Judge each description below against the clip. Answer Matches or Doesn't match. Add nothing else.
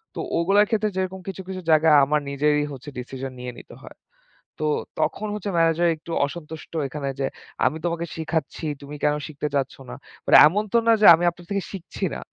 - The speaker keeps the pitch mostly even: Doesn't match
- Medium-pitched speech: Matches